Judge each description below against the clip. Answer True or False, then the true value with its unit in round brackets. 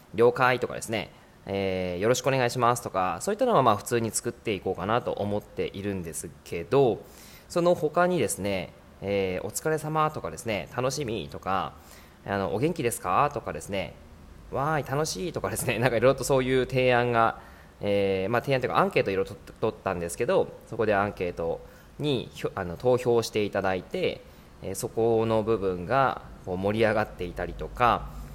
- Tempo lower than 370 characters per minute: False (375 characters per minute)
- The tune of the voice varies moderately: True (5.0 semitones)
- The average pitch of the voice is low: True (105 Hz)